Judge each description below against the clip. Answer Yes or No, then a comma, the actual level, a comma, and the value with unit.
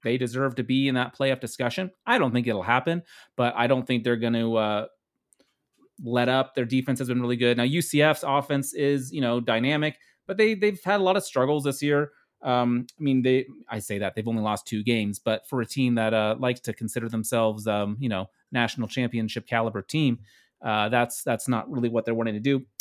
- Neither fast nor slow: No, fast, 225 wpm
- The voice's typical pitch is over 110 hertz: Yes, low, 125 Hz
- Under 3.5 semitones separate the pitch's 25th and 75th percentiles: Yes, average, 3.0 semitones